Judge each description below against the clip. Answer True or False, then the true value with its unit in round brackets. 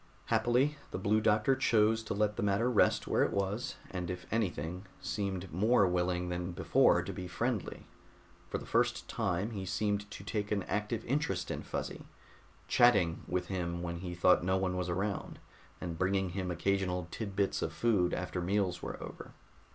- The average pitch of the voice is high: False (95 Hz)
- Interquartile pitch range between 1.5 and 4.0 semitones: True (2.9 semitones)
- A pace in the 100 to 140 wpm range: False (180 wpm)